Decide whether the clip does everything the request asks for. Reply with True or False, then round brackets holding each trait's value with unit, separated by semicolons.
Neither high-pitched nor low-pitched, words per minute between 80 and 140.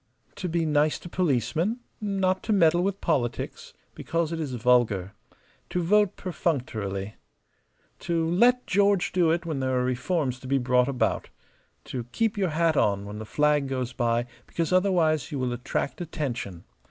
False (155 Hz; 165 wpm)